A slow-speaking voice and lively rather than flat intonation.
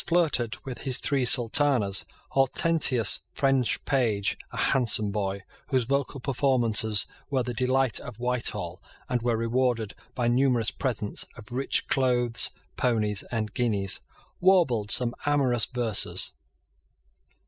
No: slow, 120 wpm; average, 3.1 semitones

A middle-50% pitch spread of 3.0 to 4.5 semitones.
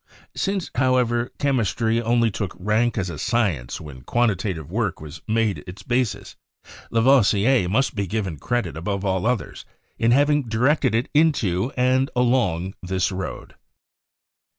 No: average, 4.9 semitones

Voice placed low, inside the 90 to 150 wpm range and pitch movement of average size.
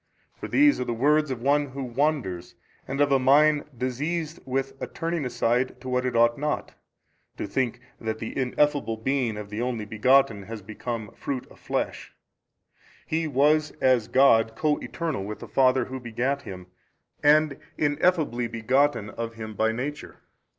No: low, 130 Hz; average, 165 wpm; average, 4.2 semitones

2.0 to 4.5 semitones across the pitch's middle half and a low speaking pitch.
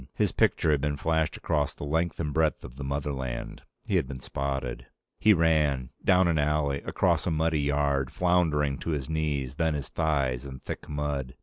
Yes: narrow, 2.5 semitones; very low, 75 Hz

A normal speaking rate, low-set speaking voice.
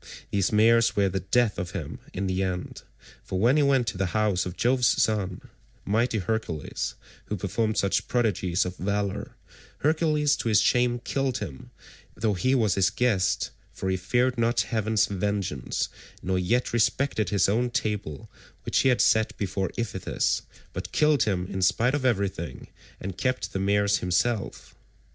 Yes: average, 165 wpm; low, 105 Hz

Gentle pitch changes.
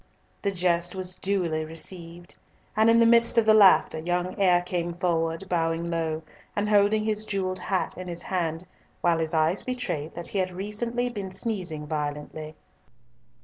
No: average, 3.6 semitones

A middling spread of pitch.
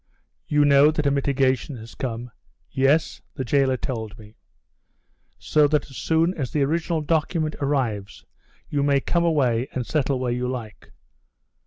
Yes: average, 3.4 semitones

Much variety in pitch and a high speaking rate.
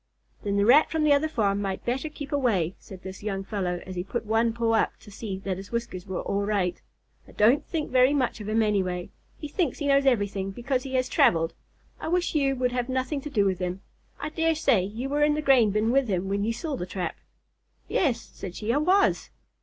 Yes: wide, 5.9 semitones; fast, 235 wpm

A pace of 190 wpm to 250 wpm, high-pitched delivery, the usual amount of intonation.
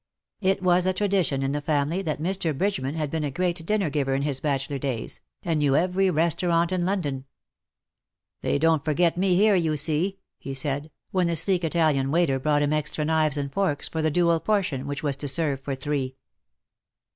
No: average, 195 wpm; medium, 155 Hz; average, 3.9 semitones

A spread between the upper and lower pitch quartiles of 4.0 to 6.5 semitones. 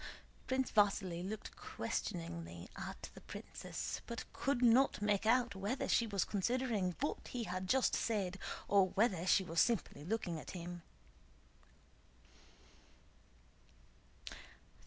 Yes: average, 4.7 semitones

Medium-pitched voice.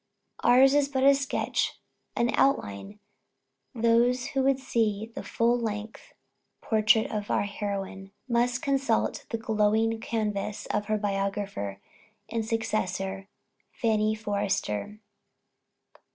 No: high, 220 Hz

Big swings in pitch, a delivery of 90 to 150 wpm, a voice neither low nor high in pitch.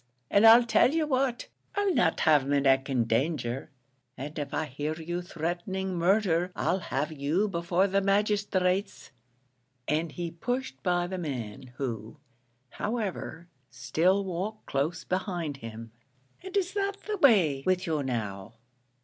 Yes: wide, 6.0 semitones; average, 145 wpm; medium, 175 Hz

